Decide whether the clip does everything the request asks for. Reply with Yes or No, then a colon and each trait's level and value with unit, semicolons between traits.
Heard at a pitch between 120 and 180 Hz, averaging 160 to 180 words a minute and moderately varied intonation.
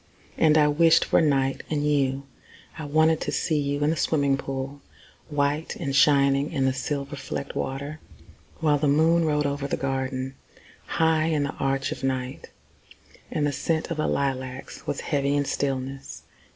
No: medium, 140 Hz; average, 170 wpm; narrow, 2.1 semitones